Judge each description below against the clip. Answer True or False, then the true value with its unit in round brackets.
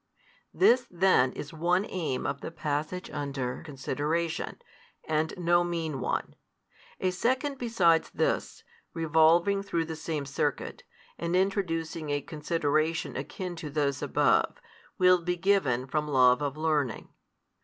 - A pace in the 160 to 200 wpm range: False (135 wpm)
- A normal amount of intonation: True (3.5 semitones)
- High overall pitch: False (160 Hz)